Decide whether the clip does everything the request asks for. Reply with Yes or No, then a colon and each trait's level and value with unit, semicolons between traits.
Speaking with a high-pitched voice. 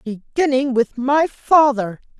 Yes: very high, 260 Hz